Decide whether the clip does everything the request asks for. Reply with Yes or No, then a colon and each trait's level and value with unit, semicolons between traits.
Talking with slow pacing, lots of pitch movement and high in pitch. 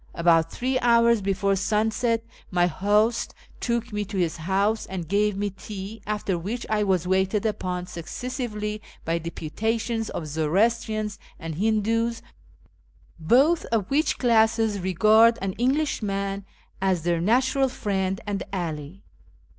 No: slow, 130 wpm; average, 3.4 semitones; high, 205 Hz